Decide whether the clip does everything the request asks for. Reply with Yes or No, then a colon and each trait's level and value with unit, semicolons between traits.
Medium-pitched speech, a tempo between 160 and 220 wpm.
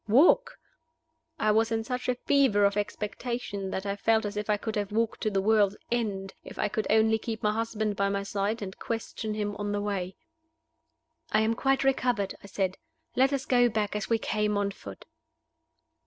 No: high, 215 Hz; average, 200 wpm